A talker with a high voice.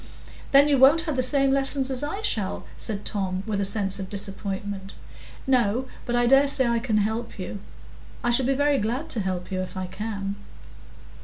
Yes: high, 225 Hz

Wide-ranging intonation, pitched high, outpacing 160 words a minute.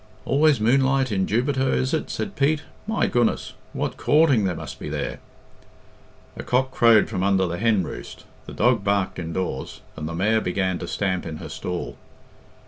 No: wide, 6.2 semitones; low, 110 Hz; average, 175 wpm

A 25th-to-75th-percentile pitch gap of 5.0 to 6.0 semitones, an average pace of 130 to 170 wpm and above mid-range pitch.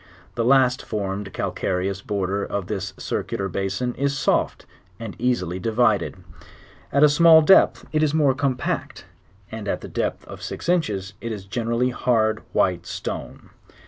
No: average, 5.3 semitones; average, 150 wpm; low, 110 Hz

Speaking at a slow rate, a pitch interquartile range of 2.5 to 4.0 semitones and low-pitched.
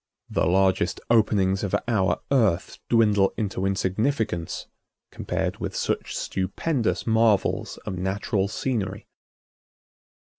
Yes: slow, 100 wpm; average, 2.9 semitones; low, 100 Hz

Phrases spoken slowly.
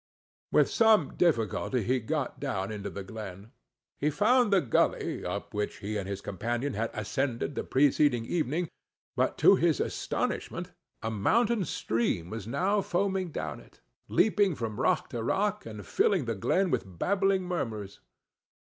No: average, 155 wpm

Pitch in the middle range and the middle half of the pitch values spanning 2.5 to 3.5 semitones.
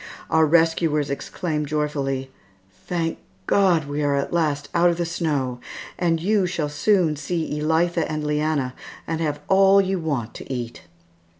Yes: medium, 155 Hz; average, 2.9 semitones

